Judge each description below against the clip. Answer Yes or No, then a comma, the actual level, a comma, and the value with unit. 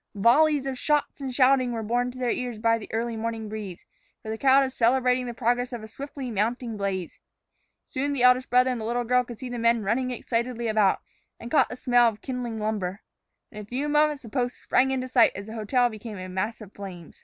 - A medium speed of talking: No, fast, 230 wpm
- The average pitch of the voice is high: Yes, high, 240 Hz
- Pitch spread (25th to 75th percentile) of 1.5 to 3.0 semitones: Yes, narrow, 2.6 semitones